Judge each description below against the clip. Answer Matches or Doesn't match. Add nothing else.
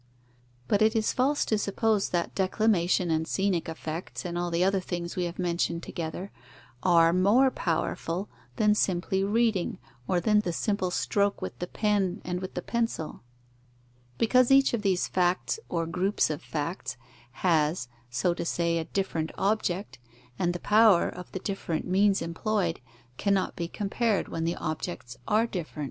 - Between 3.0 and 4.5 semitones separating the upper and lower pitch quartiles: Matches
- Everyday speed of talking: Matches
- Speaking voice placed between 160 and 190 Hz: Matches